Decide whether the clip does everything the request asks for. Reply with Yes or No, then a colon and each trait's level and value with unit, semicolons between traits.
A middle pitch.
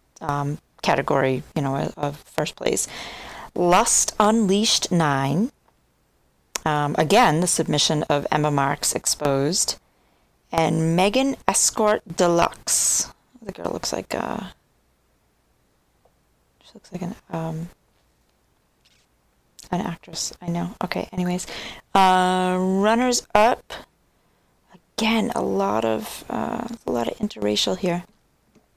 Yes: medium, 165 Hz